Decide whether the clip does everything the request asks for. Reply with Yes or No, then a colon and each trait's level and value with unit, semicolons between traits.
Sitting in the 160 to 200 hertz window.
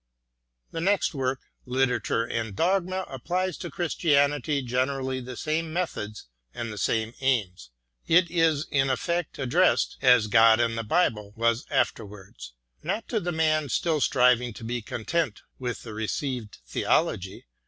No: low, 130 Hz